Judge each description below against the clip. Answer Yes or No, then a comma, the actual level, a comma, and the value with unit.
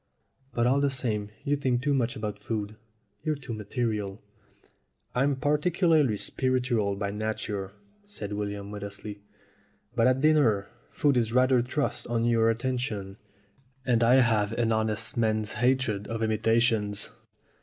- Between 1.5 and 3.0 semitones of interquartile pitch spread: No, average, 3.7 semitones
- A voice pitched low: Yes, low, 115 Hz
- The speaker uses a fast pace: No, slow, 135 wpm